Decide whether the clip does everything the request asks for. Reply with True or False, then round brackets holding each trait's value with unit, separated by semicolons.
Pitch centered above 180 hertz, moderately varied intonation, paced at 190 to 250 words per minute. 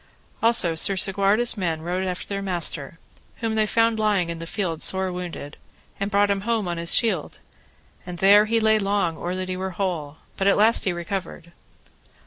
True (190 Hz; 3.2 semitones; 195 wpm)